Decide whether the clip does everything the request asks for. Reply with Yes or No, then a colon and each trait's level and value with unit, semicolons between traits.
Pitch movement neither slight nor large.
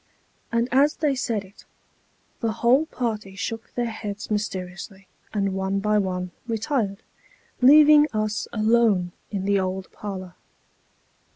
Yes: average, 3.5 semitones